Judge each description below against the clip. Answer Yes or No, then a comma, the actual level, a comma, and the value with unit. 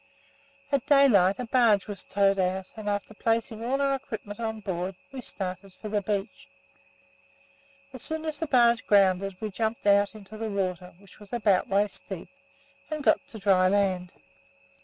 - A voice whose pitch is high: Yes, high, 205 Hz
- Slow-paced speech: No, average, 170 wpm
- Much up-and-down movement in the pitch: No, average, 3.3 semitones